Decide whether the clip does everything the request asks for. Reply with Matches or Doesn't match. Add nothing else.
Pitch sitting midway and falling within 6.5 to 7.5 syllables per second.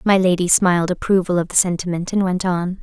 Doesn't match